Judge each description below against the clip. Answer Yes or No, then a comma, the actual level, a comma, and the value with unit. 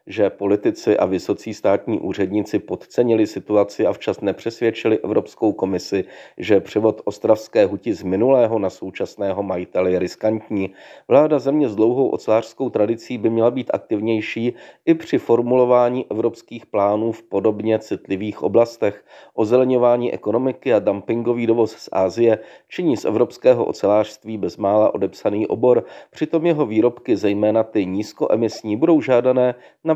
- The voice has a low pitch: Yes, low, 115 Hz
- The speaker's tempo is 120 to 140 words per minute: Yes, average, 130 wpm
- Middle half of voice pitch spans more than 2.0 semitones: Yes, average, 2.7 semitones